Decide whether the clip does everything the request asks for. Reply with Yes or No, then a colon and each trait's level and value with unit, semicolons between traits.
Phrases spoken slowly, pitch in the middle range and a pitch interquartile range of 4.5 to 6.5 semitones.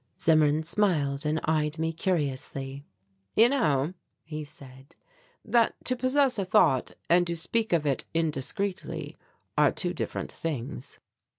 Yes: slow, 130 wpm; medium, 160 Hz; average, 4.8 semitones